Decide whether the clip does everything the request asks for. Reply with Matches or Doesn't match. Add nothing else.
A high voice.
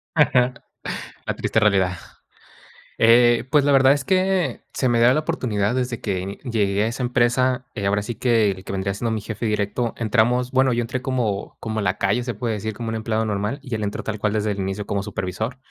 Doesn't match